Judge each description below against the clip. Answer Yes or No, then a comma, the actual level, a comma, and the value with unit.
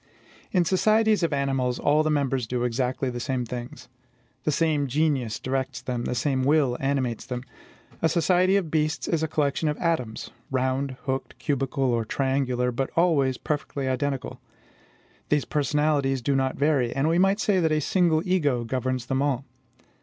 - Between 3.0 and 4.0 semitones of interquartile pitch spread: Yes, average, 3.3 semitones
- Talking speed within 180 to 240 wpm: No, average, 170 wpm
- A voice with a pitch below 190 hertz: Yes, medium, 140 Hz